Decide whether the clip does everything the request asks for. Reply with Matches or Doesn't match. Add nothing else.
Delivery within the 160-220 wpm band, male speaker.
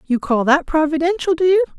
Doesn't match